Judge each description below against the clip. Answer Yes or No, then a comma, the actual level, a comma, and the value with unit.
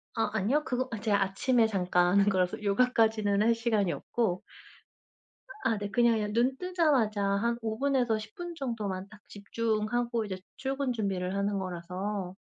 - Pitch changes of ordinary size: Yes, average, 3.2 semitones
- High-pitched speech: Yes, high, 215 Hz